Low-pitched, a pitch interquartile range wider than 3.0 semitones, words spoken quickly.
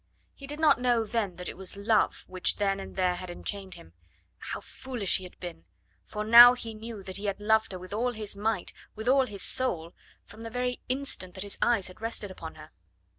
No: high, 205 Hz; average, 4.0 semitones; fast, 230 wpm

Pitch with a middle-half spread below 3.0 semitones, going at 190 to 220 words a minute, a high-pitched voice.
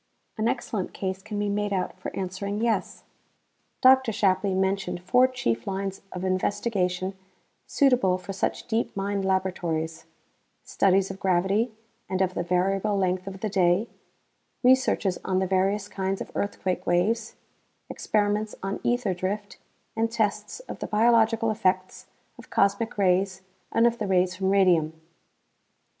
No: narrow, 2.5 semitones; average, 145 wpm; high, 195 Hz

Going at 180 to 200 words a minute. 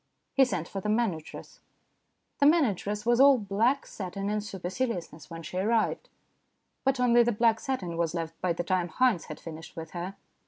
Yes: average, 185 wpm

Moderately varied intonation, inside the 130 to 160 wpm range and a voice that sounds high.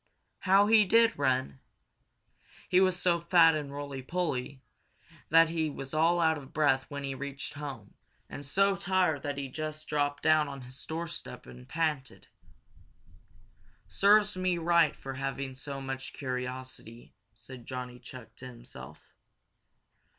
No: average, 4.2 semitones; average, 145 wpm; medium, 145 Hz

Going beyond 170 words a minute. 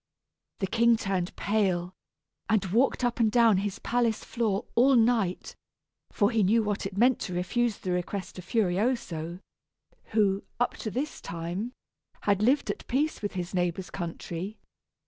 No: average, 155 wpm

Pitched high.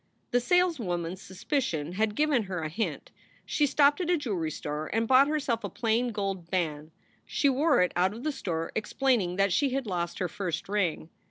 Yes: high, 210 Hz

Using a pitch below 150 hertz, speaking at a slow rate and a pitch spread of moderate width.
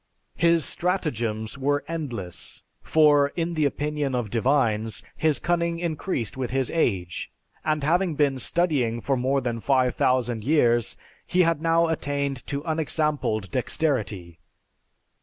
Yes: medium, 140 Hz; slow, 125 wpm; average, 5.0 semitones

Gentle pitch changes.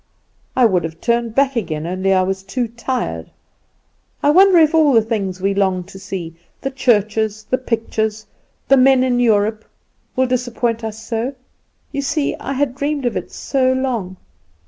No: average, 4.7 semitones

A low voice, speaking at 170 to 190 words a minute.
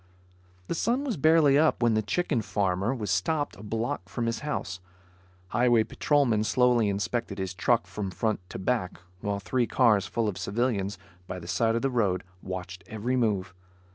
Yes: low, 110 Hz; average, 175 wpm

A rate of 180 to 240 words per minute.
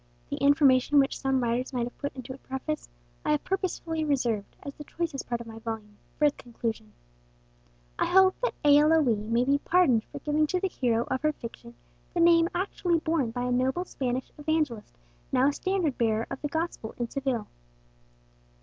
Yes: average, 195 wpm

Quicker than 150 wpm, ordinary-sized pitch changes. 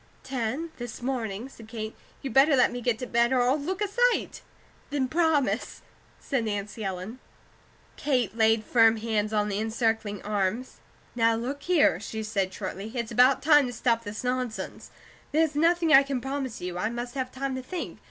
Yes: average, 180 wpm; average, 3.8 semitones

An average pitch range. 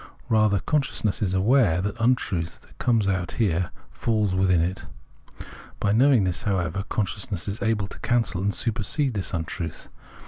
Yes: average, 3.6 semitones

